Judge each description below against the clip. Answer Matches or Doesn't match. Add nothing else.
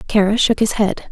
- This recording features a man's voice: Doesn't match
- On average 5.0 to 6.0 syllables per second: Matches